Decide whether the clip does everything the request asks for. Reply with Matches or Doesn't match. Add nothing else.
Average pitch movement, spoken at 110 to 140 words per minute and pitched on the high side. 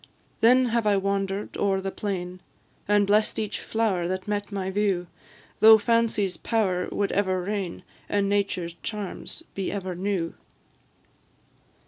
Doesn't match